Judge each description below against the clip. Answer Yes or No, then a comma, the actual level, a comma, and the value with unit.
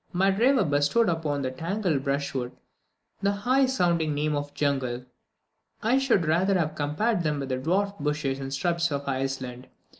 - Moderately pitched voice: Yes, medium, 155 Hz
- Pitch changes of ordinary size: No, wide, 5.8 semitones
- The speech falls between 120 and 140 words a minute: No, average, 160 wpm